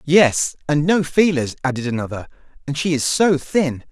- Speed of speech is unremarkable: Yes, average, 170 wpm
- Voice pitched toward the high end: No, medium, 150 Hz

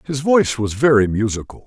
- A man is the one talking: Yes, male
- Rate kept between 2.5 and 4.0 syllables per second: No, 5.7 syllables/s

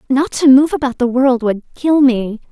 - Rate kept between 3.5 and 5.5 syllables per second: Yes, 4.7 syllables/s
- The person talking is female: Yes, female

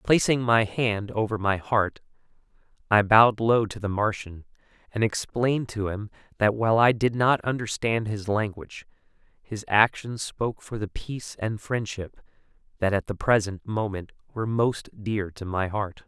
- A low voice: Yes, low, 110 Hz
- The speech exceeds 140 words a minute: Yes, average, 160 wpm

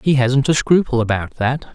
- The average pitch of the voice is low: Yes, low, 130 Hz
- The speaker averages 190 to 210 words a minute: Yes, fast, 205 wpm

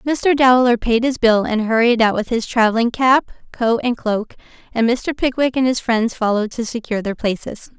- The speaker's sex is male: No, female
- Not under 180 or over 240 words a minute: Yes, average, 200 wpm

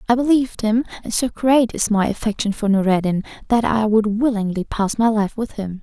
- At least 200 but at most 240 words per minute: Yes, fast, 205 wpm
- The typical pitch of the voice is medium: No, high, 220 Hz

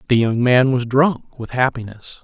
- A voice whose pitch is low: Yes, low, 125 Hz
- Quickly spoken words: No, average, 190 wpm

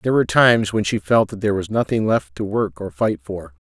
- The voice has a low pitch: Yes, low, 110 Hz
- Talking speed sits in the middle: No, fast, 260 wpm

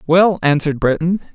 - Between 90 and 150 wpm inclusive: Yes, slow, 135 wpm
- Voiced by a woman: No, male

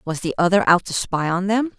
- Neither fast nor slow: No, fast, 270 wpm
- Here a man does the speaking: No, female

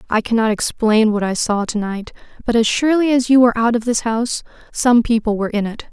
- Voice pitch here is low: No, high, 225 Hz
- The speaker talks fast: Yes, fast, 235 wpm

